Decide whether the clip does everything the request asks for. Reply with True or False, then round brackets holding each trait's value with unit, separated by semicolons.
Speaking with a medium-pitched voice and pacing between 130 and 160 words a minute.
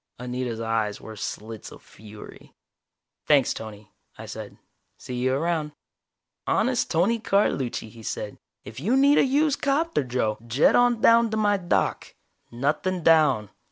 True (145 Hz; 145 wpm)